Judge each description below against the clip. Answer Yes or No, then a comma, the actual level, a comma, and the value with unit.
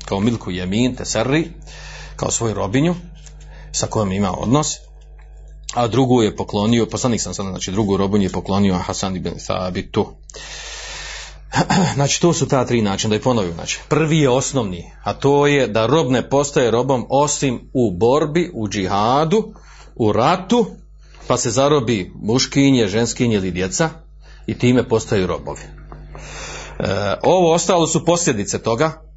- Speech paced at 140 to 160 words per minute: Yes, average, 145 wpm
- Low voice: Yes, low, 120 Hz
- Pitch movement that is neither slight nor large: No, wide, 7.5 semitones